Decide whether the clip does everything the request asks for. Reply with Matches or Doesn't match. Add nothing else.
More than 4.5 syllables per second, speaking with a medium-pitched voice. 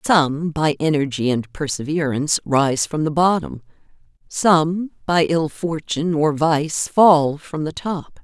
Doesn't match